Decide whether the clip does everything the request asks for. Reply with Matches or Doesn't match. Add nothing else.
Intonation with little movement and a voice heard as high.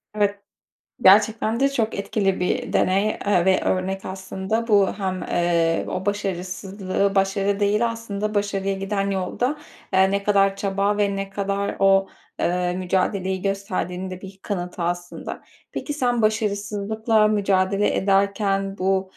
Matches